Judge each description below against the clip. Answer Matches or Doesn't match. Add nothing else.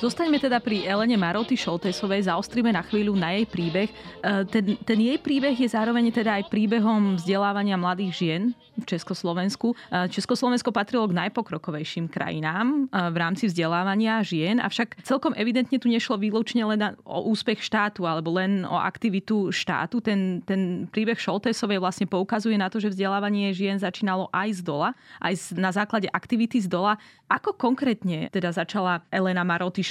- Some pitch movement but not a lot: Matches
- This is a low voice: Doesn't match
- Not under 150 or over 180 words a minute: Matches